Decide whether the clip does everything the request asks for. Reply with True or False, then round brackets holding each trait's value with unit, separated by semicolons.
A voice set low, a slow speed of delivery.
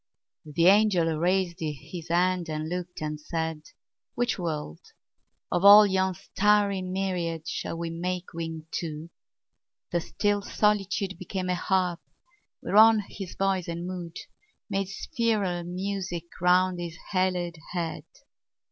False (180 Hz; 125 wpm)